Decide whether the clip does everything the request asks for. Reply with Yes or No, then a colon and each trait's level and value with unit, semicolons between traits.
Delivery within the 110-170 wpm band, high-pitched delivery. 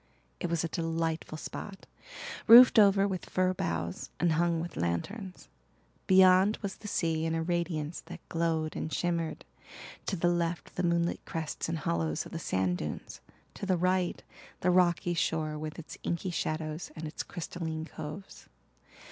No: average, 160 wpm; medium, 170 Hz